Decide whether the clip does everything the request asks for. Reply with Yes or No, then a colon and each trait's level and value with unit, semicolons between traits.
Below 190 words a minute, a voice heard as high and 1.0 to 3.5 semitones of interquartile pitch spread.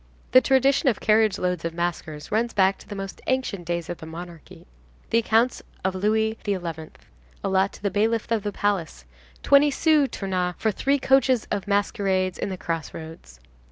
No: average, 175 wpm; high, 200 Hz; average, 4.4 semitones